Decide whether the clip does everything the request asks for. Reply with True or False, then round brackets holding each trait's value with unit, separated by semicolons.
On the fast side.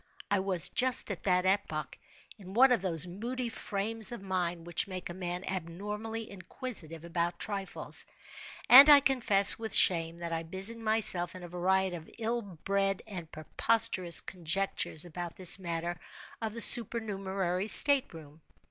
False (155 wpm)